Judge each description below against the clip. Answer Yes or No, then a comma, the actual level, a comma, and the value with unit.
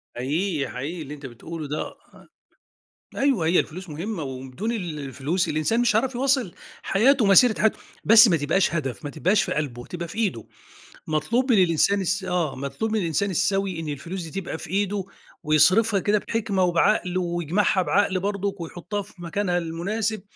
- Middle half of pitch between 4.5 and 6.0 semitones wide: Yes, average, 4.8 semitones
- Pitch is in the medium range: Yes, medium, 180 Hz